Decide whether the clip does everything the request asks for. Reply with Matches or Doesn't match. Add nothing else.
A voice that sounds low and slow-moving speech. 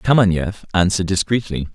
Matches